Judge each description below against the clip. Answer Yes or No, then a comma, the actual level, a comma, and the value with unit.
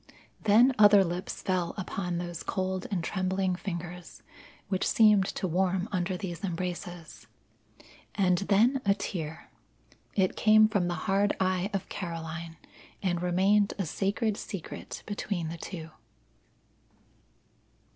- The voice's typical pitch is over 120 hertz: Yes, medium, 185 Hz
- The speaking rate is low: Yes, slow, 125 wpm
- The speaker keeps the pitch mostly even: Yes, narrow, 2.3 semitones